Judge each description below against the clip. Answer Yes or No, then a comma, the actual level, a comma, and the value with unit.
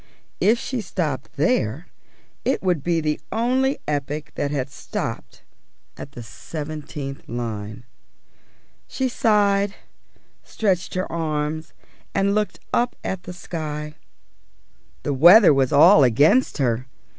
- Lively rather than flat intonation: Yes, wide, 6.0 semitones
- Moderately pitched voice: Yes, medium, 155 Hz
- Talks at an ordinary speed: No, slow, 120 wpm